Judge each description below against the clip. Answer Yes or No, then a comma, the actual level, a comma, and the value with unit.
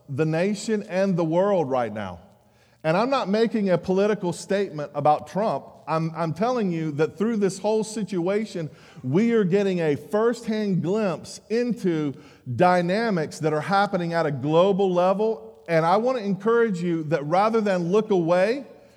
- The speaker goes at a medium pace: Yes, average, 160 wpm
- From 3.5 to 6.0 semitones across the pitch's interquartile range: Yes, average, 5.0 semitones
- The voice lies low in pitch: No, medium, 185 Hz